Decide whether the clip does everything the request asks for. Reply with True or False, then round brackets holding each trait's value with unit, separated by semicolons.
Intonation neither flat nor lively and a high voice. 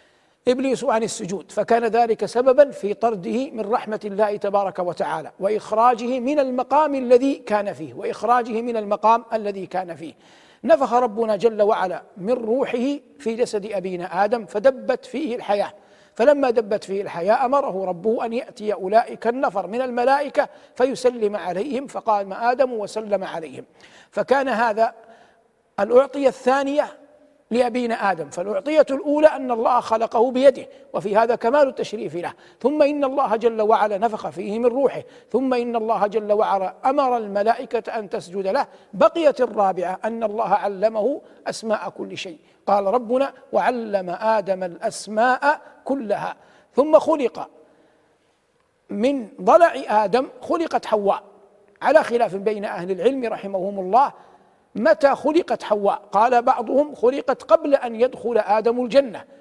True (4.2 semitones; 230 Hz)